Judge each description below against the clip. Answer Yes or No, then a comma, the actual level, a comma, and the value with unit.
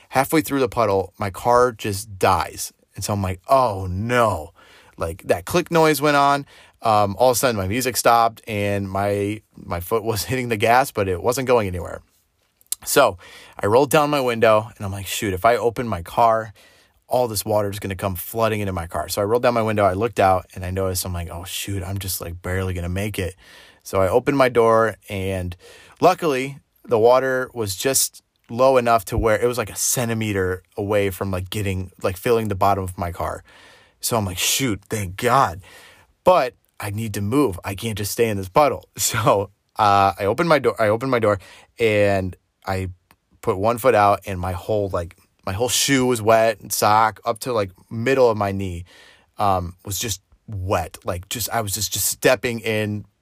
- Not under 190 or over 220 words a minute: Yes, fast, 205 wpm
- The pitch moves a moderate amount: Yes, average, 3.4 semitones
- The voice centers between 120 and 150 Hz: No, low, 105 Hz